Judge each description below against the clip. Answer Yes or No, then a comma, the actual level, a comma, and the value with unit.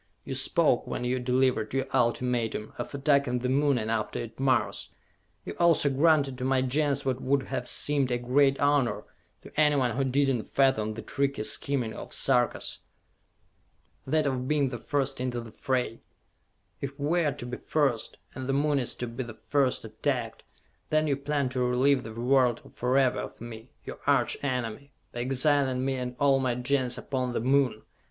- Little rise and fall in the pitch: Yes, narrow, 2.3 semitones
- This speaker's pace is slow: No, average, 185 wpm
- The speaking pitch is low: Yes, low, 130 Hz